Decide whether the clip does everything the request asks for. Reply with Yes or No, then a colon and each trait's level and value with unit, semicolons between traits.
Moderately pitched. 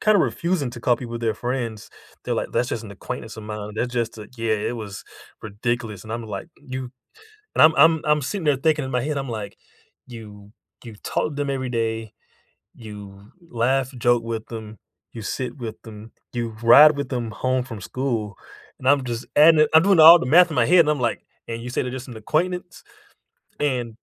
No: low, 120 Hz